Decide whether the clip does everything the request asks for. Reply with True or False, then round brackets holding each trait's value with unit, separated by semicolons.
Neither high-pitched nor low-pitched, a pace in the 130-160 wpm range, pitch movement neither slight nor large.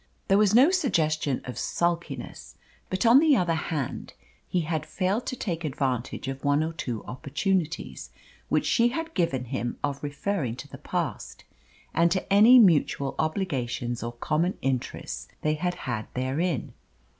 False (155 Hz; 155 wpm; 6.1 semitones)